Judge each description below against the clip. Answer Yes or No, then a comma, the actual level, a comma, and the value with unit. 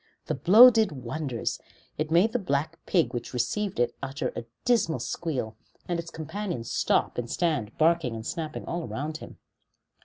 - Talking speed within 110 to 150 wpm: No, average, 165 wpm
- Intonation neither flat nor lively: No, wide, 5.7 semitones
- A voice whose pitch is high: No, medium, 155 Hz